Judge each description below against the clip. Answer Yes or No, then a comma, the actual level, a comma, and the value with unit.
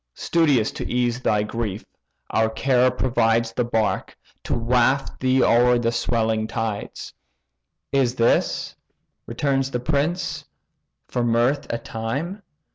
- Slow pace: Yes, slow, 120 wpm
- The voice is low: Yes, low, 120 Hz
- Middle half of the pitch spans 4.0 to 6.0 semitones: No, narrow, 2.6 semitones